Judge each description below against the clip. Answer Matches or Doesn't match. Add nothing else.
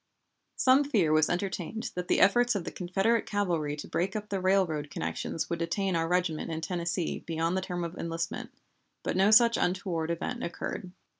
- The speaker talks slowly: Doesn't match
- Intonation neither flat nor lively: Matches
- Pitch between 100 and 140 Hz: Doesn't match